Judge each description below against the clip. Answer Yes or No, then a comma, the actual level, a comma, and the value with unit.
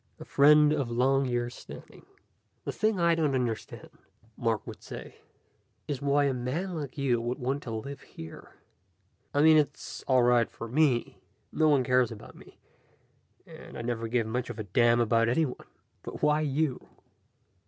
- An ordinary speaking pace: Yes, average, 165 wpm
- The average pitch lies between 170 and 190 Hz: No, low, 130 Hz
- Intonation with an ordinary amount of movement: Yes, average, 3.7 semitones